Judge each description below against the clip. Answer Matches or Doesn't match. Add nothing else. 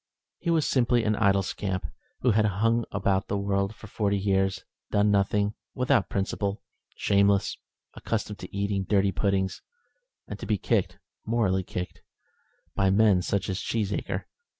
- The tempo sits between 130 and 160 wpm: Matches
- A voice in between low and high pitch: Doesn't match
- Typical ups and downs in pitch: Doesn't match